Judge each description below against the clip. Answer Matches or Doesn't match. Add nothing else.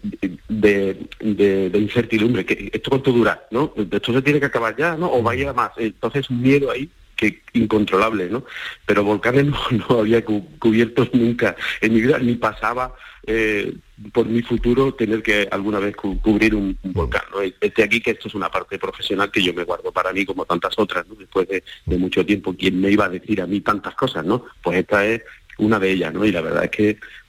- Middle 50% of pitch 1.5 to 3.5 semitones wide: Matches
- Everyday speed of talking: Doesn't match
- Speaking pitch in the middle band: Doesn't match